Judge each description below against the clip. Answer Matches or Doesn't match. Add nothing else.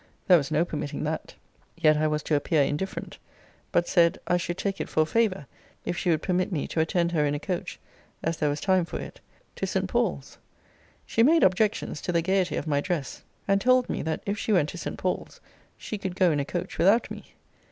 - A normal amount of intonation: Matches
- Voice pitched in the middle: Matches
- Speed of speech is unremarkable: Doesn't match